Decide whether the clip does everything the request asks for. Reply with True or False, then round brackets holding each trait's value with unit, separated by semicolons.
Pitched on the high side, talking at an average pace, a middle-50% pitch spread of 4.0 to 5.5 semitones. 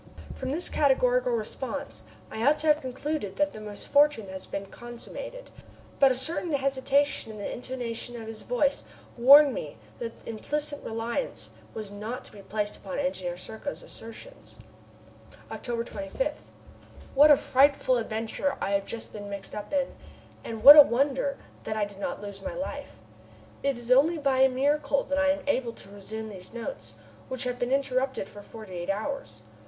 True (255 Hz; 170 wpm; 4.7 semitones)